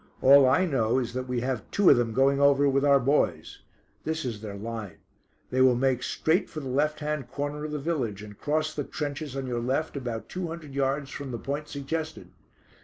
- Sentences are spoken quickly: Yes, fast, 215 wpm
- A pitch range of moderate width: Yes, average, 3.2 semitones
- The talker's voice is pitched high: No, medium, 140 Hz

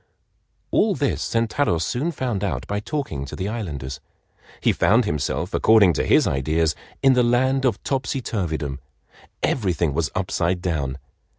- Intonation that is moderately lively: No, wide, 7.7 semitones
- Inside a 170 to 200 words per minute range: No, average, 140 wpm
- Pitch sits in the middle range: No, low, 100 Hz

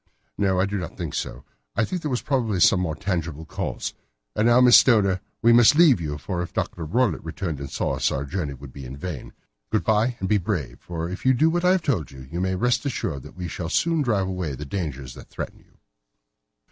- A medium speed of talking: No, fast, 245 wpm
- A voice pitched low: Yes, very low, 95 Hz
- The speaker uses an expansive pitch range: Yes, wide, 6.8 semitones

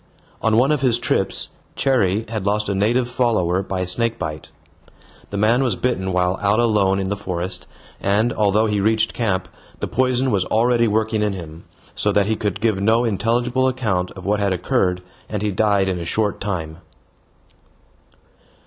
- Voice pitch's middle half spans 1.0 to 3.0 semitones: No, average, 3.4 semitones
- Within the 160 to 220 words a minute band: Yes, average, 175 wpm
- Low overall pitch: Yes, low, 105 Hz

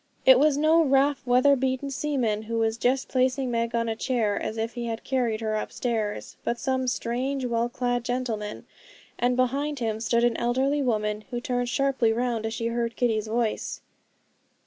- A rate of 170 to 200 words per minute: Yes, average, 180 wpm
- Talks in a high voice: Yes, high, 240 Hz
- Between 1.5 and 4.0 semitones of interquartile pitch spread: Yes, narrow, 2.4 semitones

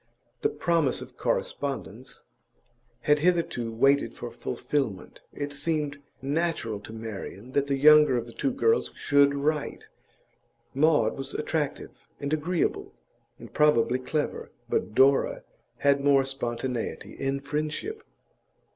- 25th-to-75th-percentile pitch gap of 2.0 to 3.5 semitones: Yes, average, 2.8 semitones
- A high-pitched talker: No, medium, 140 Hz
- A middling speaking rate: No, slow, 120 wpm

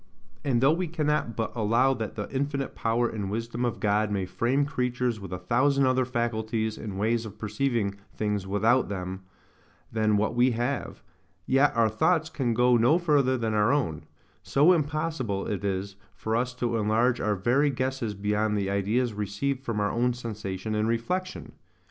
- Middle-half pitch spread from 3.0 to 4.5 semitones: Yes, average, 3.8 semitones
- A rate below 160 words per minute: No, average, 175 wpm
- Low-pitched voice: Yes, low, 115 Hz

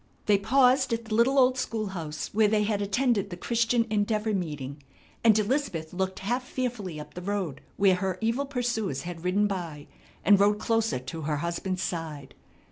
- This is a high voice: Yes, high, 205 Hz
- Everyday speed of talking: Yes, average, 180 wpm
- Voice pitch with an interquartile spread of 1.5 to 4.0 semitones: No, average, 4.7 semitones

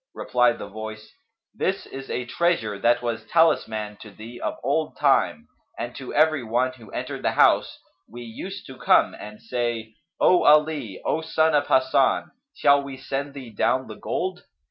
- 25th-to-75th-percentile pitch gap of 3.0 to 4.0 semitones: No, average, 4.8 semitones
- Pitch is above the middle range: No, low, 130 Hz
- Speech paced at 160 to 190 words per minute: Yes, average, 170 wpm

